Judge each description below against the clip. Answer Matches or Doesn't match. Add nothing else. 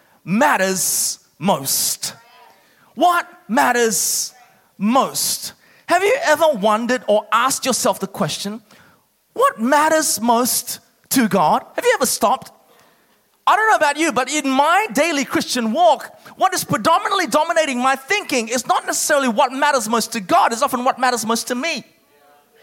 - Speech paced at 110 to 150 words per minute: Matches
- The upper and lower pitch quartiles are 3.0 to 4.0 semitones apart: Doesn't match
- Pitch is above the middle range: Matches